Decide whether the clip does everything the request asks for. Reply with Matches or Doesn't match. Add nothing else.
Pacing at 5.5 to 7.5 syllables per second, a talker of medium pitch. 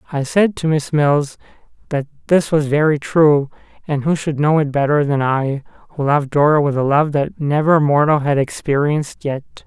Doesn't match